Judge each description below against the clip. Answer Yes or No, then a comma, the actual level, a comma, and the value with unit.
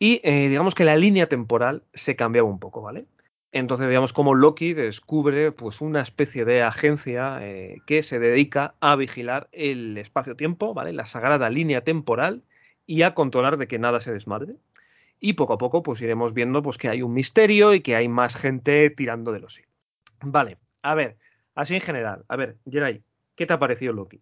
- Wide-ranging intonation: No, average, 4.2 semitones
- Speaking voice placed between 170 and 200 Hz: No, low, 135 Hz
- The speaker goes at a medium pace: No, fast, 195 wpm